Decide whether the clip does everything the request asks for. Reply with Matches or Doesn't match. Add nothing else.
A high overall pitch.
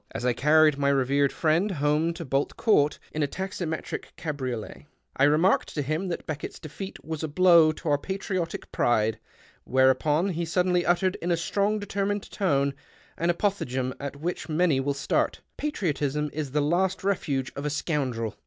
Doesn't match